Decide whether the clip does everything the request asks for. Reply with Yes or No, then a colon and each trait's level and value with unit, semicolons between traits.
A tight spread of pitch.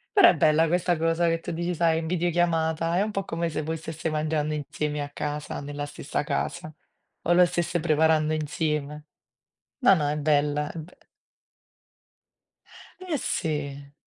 Yes: narrow, 2.2 semitones